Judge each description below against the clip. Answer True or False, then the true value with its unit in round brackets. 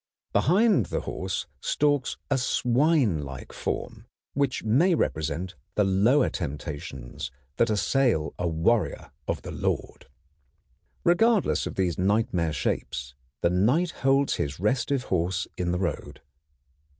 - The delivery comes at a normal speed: False (120 wpm)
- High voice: False (100 Hz)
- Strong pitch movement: True (8.5 semitones)